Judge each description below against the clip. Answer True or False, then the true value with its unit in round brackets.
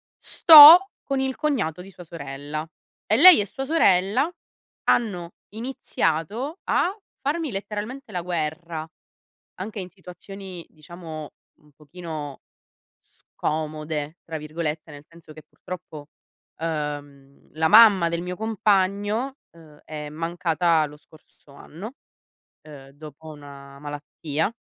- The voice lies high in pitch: False (170 Hz)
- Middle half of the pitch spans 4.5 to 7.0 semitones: True (5.3 semitones)